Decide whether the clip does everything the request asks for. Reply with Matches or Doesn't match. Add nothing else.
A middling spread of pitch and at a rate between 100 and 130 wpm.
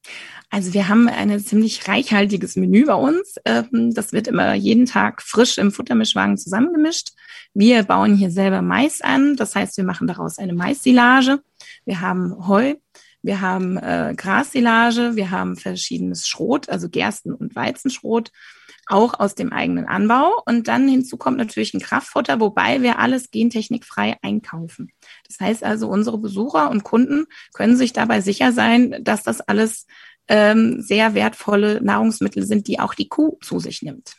Doesn't match